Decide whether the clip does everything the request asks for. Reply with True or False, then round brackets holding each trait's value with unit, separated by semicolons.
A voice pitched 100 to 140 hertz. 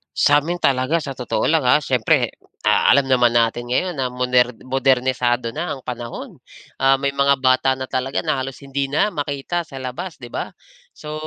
True (135 Hz)